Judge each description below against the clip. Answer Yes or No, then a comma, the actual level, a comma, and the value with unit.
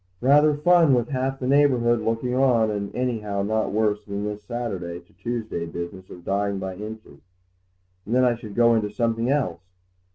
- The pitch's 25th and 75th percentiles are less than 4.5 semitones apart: Yes, average, 3.7 semitones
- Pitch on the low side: Yes, low, 115 Hz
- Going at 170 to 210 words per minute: Yes, average, 185 wpm